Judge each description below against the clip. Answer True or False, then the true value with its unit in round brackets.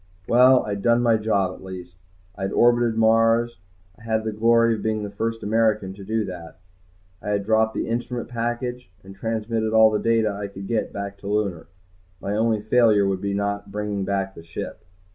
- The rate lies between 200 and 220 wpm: True (205 wpm)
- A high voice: False (110 Hz)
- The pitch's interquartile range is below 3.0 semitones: True (2.4 semitones)